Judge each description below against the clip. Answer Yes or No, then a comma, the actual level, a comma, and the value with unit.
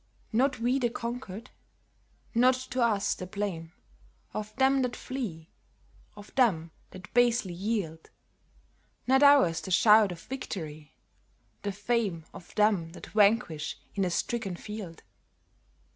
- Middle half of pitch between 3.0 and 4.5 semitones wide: No, average, 5.3 semitones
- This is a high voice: Yes, high, 210 Hz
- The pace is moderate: No, slow, 130 wpm